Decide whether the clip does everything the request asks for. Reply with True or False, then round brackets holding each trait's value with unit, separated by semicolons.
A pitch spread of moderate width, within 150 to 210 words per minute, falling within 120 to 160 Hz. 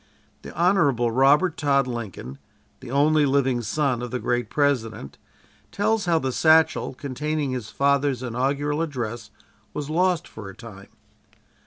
False (3.9 semitones; 140 wpm; 140 Hz)